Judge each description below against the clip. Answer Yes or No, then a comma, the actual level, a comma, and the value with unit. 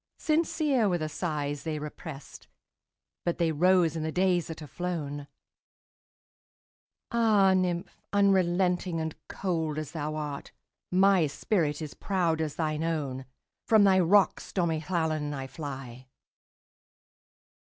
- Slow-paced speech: Yes, slow, 110 wpm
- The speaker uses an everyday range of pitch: Yes, average, 3.6 semitones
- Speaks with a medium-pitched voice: Yes, medium, 165 Hz